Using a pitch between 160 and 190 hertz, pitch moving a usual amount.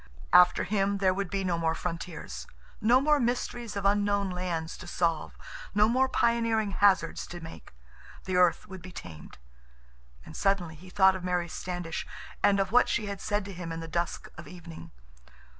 Yes: medium, 185 Hz; average, 3.0 semitones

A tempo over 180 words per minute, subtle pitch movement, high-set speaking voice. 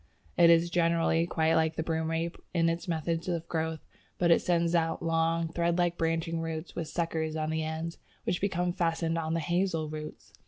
No: average, 190 wpm; narrow, 0.9 semitones; medium, 165 Hz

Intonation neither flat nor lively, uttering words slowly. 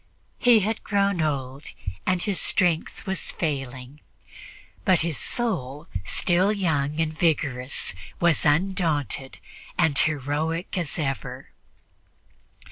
Yes: average, 4.6 semitones; slow, 105 wpm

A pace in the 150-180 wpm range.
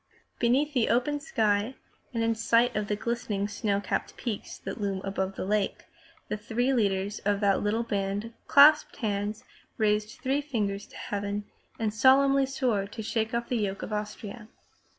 Yes: average, 170 wpm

